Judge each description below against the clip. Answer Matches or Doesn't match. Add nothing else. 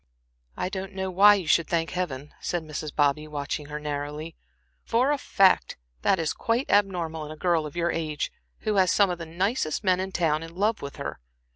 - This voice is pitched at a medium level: Matches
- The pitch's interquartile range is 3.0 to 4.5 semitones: Matches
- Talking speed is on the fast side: Matches